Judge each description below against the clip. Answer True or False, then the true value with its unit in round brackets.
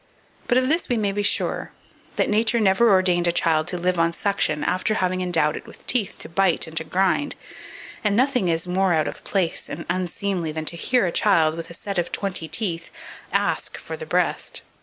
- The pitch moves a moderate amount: True (3.5 semitones)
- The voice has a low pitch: False (185 Hz)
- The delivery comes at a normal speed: False (210 wpm)